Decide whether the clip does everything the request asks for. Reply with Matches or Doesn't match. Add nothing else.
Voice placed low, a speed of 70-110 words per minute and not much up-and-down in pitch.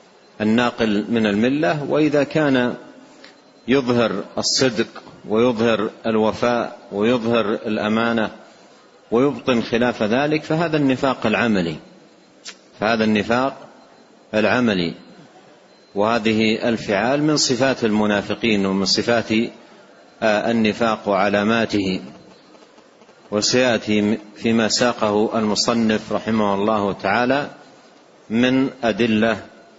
Matches